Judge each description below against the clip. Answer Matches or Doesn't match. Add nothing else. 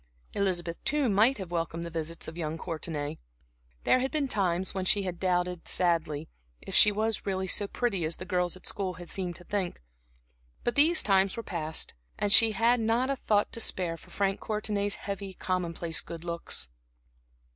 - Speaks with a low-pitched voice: Doesn't match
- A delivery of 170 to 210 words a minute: Matches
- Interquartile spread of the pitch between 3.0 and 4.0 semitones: Matches